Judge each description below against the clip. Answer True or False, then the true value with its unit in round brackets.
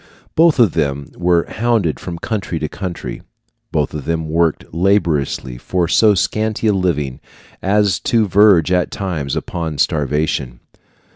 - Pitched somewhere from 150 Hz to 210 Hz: False (85 Hz)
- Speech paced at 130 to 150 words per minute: True (140 wpm)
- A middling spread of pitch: True (4.8 semitones)